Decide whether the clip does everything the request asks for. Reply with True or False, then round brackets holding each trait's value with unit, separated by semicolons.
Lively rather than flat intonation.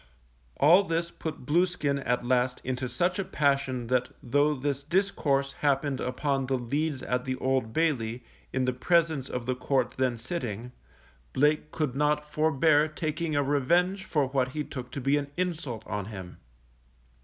False (3.4 semitones)